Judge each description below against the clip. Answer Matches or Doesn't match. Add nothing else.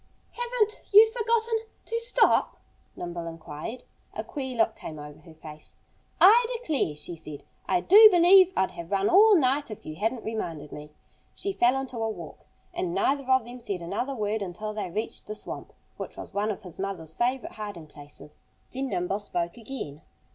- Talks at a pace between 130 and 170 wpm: Doesn't match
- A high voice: Matches